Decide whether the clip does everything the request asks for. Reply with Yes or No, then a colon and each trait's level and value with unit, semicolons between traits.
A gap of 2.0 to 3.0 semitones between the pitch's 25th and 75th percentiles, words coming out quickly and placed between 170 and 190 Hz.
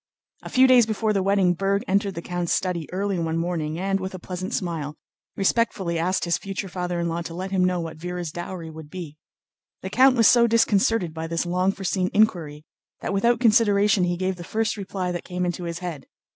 Yes: average, 2.7 semitones; fast, 215 wpm; medium, 185 Hz